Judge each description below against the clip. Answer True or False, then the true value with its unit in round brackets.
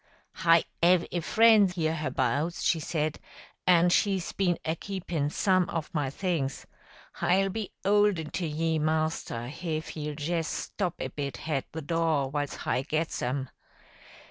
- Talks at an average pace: True (145 wpm)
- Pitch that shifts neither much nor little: True (3.2 semitones)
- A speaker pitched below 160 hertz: False (165 Hz)